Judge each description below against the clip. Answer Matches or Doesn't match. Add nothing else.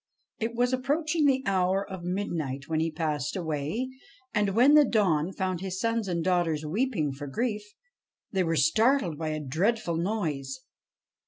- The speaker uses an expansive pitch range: Matches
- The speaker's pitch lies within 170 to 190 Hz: Matches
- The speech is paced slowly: Doesn't match